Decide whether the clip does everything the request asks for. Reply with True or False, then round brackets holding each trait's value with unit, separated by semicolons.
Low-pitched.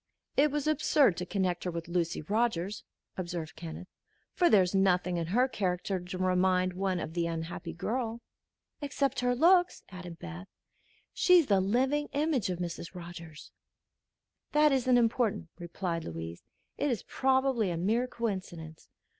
False (185 Hz)